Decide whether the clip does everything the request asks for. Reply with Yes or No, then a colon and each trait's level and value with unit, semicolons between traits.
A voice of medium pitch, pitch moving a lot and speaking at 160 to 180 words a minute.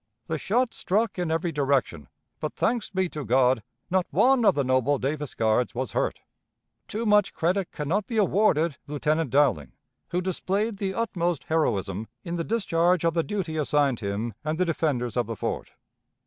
Yes: medium, 160 Hz; wide, 6.3 semitones; average, 175 wpm